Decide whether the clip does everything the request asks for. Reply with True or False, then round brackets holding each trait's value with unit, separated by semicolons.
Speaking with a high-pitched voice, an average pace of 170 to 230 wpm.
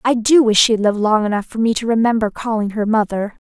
False (220 Hz; 240 wpm)